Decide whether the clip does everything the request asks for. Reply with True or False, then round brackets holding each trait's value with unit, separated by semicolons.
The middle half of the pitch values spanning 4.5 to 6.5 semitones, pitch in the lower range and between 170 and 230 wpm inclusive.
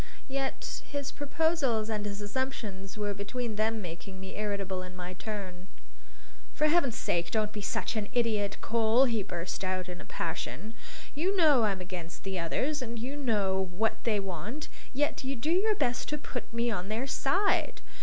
False (5.6 semitones; 220 Hz; 175 wpm)